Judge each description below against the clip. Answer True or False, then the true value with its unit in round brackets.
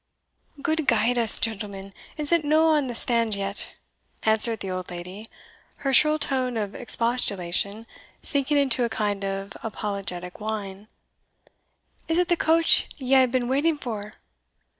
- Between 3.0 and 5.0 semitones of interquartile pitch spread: False (5.4 semitones)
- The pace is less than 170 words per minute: True (145 wpm)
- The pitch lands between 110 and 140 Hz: False (230 Hz)